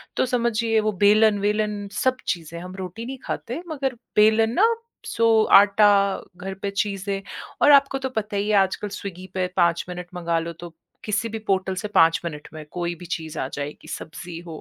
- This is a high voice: Yes, high, 200 Hz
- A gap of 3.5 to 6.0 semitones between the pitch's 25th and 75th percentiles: Yes, average, 3.9 semitones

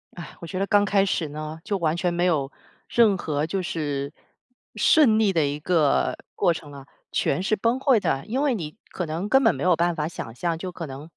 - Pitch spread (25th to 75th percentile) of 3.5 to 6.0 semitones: Yes, average, 4.6 semitones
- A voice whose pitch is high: No, medium, 170 Hz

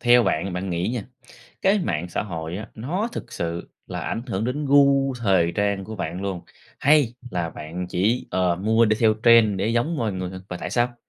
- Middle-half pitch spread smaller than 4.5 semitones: No, average, 5.1 semitones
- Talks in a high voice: No, low, 105 Hz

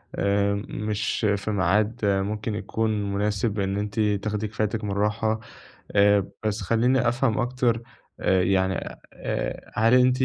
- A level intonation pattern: Yes, narrow, 1.9 semitones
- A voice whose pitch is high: No, low, 105 Hz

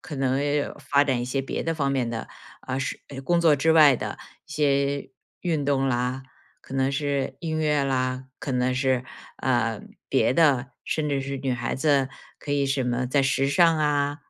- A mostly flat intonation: Yes, narrow, 1.9 semitones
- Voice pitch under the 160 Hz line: Yes, low, 135 Hz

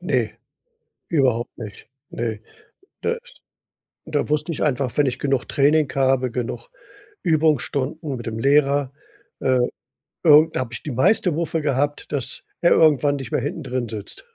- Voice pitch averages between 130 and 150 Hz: Yes, medium, 140 Hz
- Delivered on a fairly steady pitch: No, average, 3.2 semitones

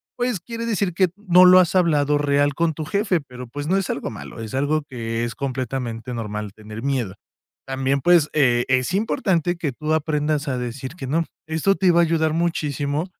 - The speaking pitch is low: No, medium, 150 Hz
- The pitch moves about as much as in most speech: Yes, average, 5.0 semitones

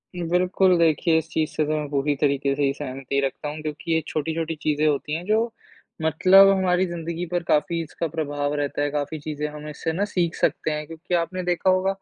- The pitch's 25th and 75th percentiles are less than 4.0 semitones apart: Yes, average, 2.9 semitones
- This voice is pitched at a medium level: Yes, medium, 160 Hz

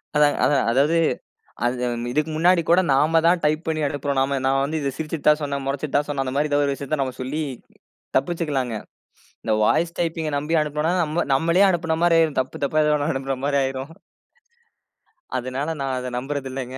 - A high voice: No, medium, 145 Hz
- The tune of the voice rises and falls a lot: No, average, 2.9 semitones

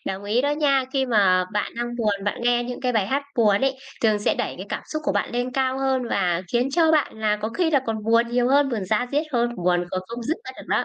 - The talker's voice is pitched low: No, high, 240 Hz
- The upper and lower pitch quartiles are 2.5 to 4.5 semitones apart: Yes, average, 4.2 semitones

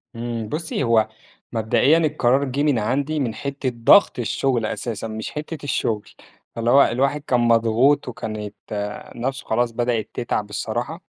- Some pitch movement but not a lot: Yes, average, 3.7 semitones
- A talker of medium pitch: No, low, 120 Hz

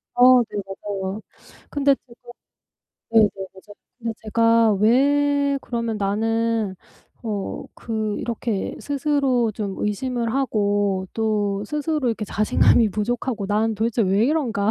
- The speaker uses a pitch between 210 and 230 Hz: Yes, high, 225 Hz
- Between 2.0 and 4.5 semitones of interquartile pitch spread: Yes, average, 3.2 semitones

